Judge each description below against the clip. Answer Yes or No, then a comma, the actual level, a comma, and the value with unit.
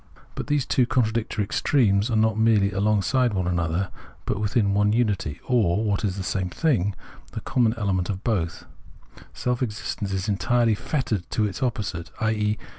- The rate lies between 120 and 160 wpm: No, average, 170 wpm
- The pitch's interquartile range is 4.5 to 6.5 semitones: No, average, 3.2 semitones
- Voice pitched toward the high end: No, low, 105 Hz